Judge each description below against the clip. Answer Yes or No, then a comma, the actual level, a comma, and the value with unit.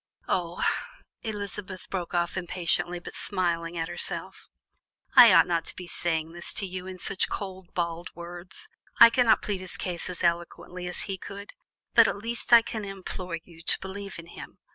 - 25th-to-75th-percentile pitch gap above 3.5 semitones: No, narrow, 2.4 semitones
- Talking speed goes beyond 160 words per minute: Yes, average, 180 wpm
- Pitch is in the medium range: Yes, medium, 180 Hz